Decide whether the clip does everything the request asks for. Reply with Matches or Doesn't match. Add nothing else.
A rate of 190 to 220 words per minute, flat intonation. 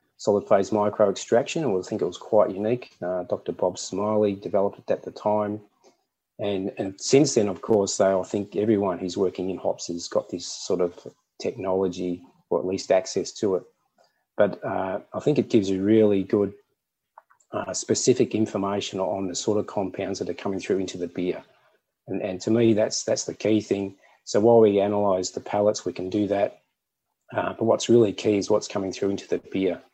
Matches